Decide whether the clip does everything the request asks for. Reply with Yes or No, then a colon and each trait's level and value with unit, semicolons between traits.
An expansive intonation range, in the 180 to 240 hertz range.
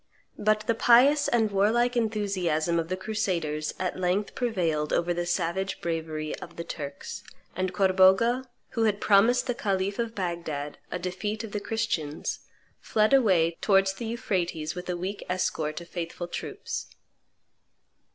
No: average, 4.2 semitones; high, 190 Hz